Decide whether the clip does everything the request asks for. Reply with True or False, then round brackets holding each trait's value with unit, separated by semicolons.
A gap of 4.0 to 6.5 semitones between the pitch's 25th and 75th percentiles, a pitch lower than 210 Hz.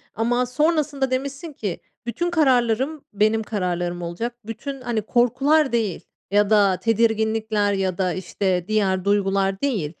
False (4.8 semitones; 220 Hz)